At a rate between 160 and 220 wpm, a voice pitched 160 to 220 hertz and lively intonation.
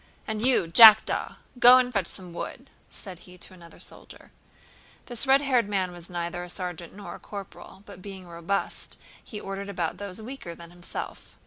No: average, 180 wpm; high, 190 Hz; average, 3.5 semitones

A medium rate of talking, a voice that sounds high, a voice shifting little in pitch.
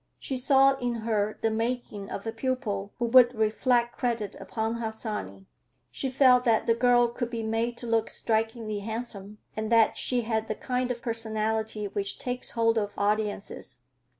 Yes: average, 170 wpm; high, 225 Hz; narrow, 2.0 semitones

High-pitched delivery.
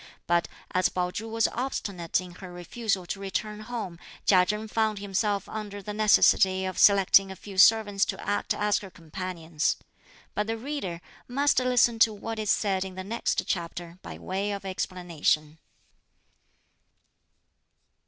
Yes: high, 195 Hz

